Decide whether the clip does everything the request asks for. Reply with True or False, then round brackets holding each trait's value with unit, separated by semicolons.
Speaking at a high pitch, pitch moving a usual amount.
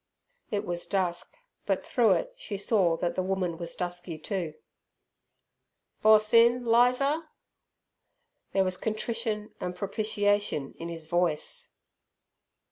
True (195 Hz; 4.0 semitones)